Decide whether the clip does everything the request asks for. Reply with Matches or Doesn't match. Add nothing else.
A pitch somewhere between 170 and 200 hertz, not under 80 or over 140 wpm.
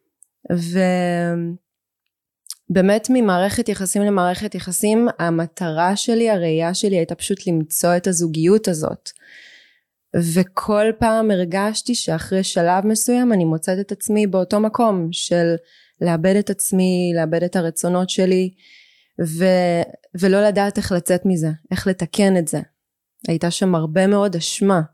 Matches